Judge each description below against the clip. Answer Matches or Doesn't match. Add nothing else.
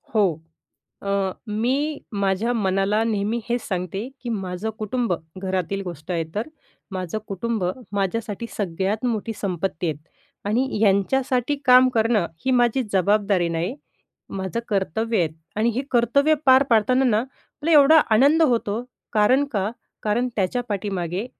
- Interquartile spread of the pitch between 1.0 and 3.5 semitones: Doesn't match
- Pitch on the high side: Matches